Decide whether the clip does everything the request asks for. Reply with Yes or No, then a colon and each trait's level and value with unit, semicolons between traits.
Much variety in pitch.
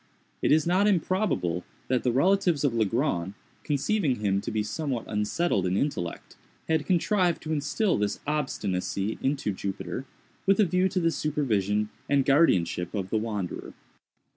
Yes: wide, 8.5 semitones